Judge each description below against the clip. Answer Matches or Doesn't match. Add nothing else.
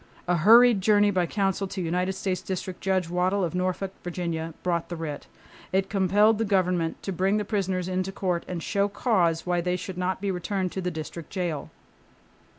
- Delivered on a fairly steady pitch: Matches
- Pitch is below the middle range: Doesn't match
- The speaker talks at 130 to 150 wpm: Doesn't match